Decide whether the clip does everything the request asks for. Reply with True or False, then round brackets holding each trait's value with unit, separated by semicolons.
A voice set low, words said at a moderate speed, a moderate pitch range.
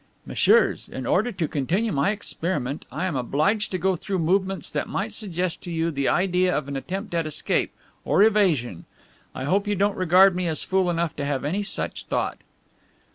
False (180 Hz; 190 wpm; 4.3 semitones)